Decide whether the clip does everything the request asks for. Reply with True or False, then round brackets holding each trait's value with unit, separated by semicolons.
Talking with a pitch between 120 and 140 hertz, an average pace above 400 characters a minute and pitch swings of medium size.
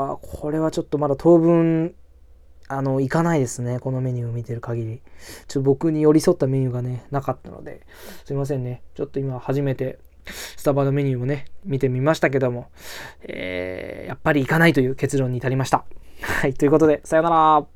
True (135 Hz; 410 characters per minute; 3.3 semitones)